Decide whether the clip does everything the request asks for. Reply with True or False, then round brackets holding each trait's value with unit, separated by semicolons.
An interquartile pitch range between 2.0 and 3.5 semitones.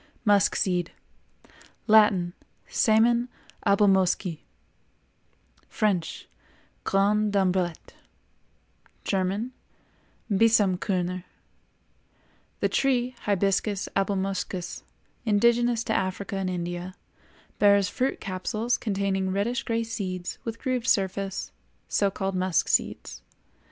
True (2.9 semitones)